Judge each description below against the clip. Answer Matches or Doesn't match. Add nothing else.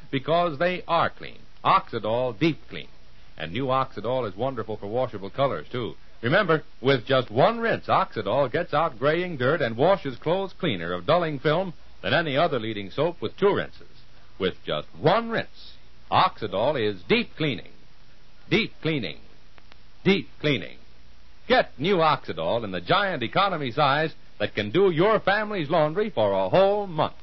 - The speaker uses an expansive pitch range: Matches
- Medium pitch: Matches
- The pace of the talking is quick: Doesn't match